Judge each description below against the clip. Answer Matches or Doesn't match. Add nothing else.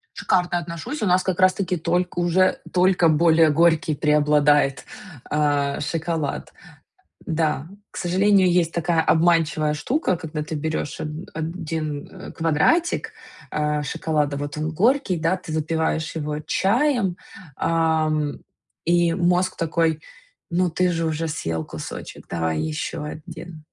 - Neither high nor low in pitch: Matches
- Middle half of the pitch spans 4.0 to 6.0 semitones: Doesn't match